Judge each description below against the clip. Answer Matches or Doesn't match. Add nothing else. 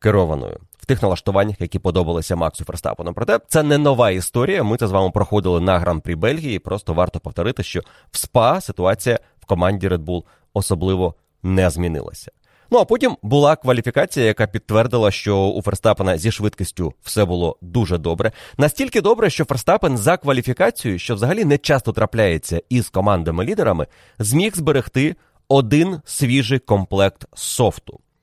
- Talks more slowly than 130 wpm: Doesn't match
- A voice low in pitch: Matches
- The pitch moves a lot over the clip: Matches